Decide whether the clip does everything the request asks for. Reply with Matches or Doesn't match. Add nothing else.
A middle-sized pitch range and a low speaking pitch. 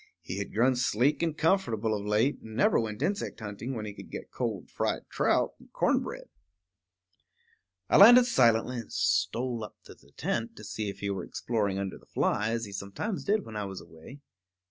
Matches